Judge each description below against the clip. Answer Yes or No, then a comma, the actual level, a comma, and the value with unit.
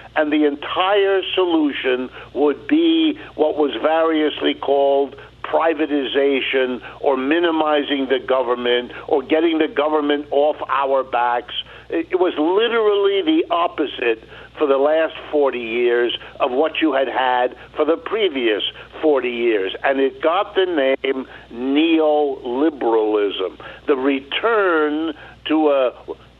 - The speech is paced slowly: Yes, slow, 120 wpm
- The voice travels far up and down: No, average, 3.7 semitones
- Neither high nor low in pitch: Yes, medium, 150 Hz